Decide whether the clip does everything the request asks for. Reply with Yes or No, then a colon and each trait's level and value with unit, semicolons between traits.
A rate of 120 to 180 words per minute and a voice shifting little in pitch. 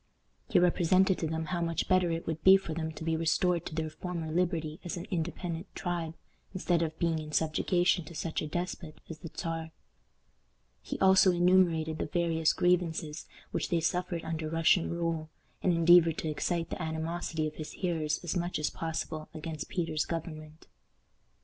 Yes: average, 175 wpm; narrow, 1.7 semitones